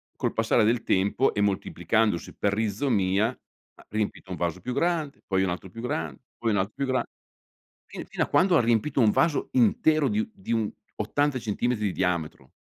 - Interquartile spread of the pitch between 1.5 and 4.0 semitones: No, average, 5.2 semitones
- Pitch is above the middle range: No, low, 110 Hz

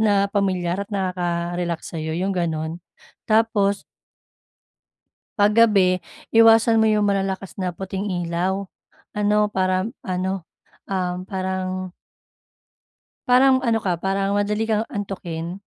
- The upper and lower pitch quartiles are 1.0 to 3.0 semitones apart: Yes, narrow, 2.4 semitones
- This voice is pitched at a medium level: No, high, 195 Hz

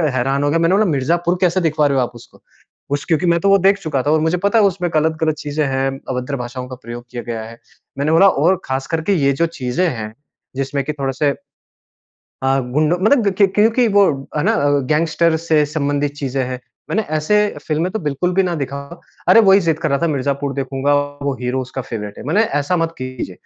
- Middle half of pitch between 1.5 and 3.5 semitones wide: No, average, 4.1 semitones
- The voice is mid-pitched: Yes, medium, 145 Hz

